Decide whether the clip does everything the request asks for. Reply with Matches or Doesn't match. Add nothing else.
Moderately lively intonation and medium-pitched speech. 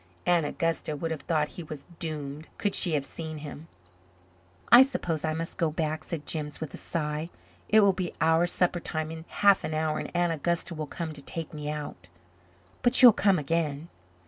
Doesn't match